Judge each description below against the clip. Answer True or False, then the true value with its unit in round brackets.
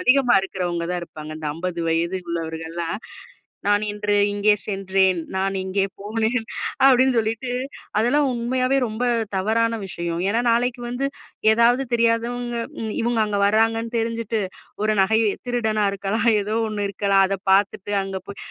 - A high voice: True (215 Hz)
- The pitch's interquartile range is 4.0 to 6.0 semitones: False (3.4 semitones)